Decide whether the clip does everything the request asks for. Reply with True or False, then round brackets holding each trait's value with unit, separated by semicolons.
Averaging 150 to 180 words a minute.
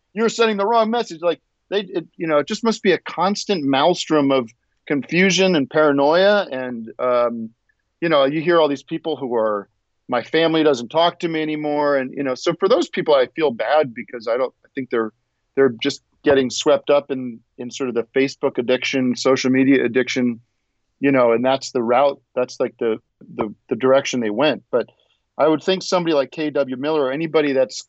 False (205 wpm)